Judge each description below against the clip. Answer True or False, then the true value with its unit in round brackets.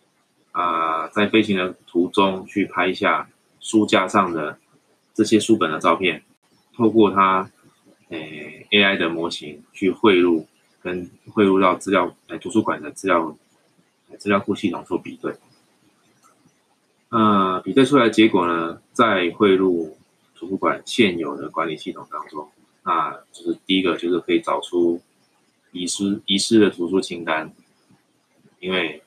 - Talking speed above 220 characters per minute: False (215 characters per minute)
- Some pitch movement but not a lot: True (3.5 semitones)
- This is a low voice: True (95 Hz)